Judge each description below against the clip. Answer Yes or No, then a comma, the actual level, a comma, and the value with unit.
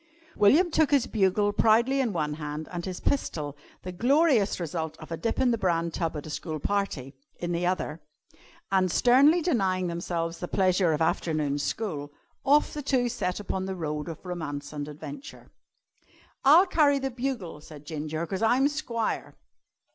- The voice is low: No, medium, 185 Hz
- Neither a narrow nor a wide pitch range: No, wide, 7.4 semitones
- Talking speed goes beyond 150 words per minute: Yes, average, 170 wpm